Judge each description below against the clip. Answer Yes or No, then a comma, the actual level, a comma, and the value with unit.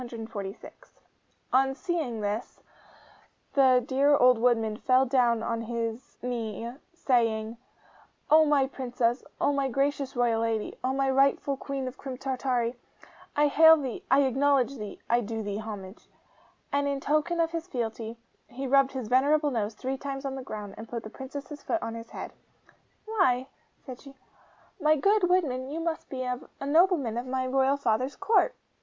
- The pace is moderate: Yes, average, 165 wpm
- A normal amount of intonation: Yes, average, 3.3 semitones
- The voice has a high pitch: Yes, very high, 260 Hz